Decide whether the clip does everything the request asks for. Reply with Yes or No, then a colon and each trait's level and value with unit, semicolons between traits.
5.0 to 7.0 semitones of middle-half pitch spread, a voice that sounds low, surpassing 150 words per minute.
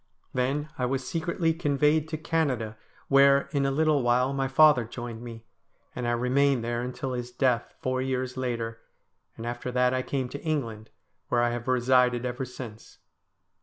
No: narrow, 2.5 semitones; low, 130 Hz; average, 170 wpm